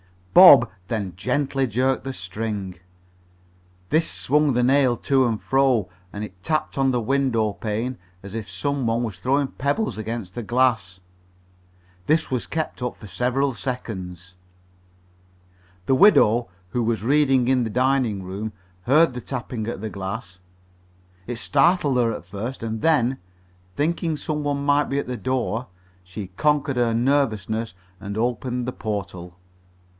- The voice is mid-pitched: No, low, 120 Hz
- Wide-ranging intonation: No, average, 4.2 semitones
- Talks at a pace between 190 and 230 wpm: No, average, 150 wpm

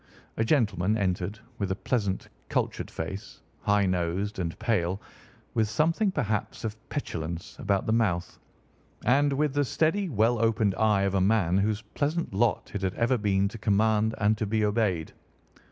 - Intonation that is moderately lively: Yes, average, 3.1 semitones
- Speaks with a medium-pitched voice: No, low, 105 Hz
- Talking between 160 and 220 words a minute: Yes, average, 165 wpm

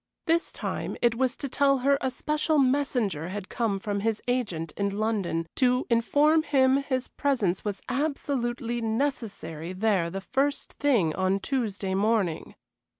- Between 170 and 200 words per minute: No, average, 150 wpm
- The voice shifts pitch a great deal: Yes, wide, 5.8 semitones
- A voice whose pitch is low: No, high, 235 Hz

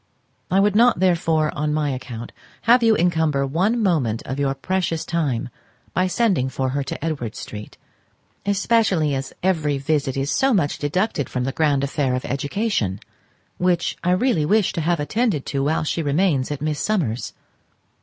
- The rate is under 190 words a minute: Yes, average, 170 wpm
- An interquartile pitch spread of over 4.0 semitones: Yes, wide, 5.4 semitones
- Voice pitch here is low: No, medium, 155 Hz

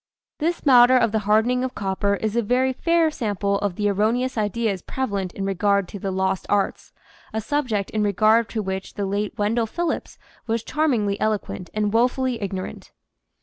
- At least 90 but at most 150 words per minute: No, average, 175 wpm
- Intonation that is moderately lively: Yes, average, 3.6 semitones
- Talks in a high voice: Yes, high, 215 Hz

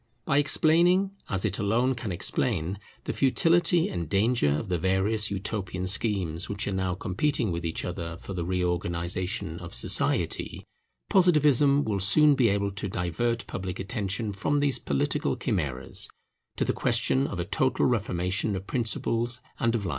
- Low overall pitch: Yes, low, 100 Hz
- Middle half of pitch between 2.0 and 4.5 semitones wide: No, wide, 5.5 semitones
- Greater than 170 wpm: No, average, 160 wpm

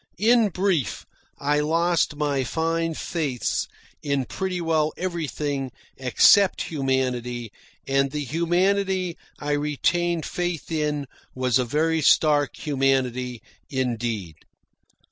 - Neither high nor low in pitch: Yes, medium, 150 Hz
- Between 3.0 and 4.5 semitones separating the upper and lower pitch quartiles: Yes, average, 4.2 semitones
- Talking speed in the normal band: No, slow, 105 wpm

